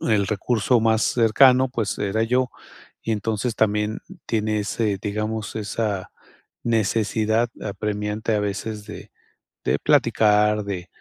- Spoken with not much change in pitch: Yes, narrow, 1.4 semitones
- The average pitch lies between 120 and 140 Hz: No, low, 110 Hz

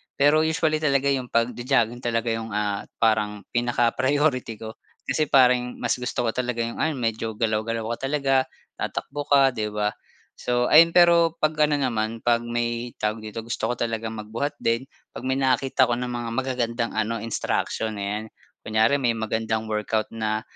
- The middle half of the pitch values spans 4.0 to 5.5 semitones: No, average, 3.0 semitones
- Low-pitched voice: Yes, low, 120 Hz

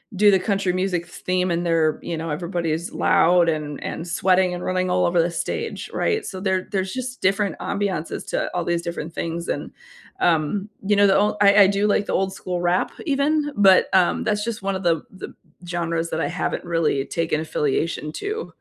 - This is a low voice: No, medium, 180 Hz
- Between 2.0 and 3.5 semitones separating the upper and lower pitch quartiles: Yes, average, 2.9 semitones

